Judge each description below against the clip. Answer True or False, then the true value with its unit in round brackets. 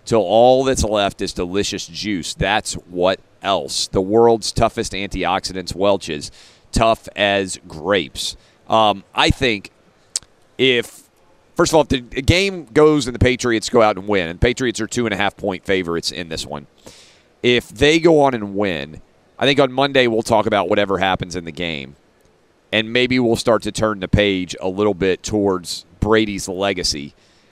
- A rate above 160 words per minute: True (175 wpm)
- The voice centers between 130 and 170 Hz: False (105 Hz)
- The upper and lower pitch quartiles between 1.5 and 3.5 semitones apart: False (4.4 semitones)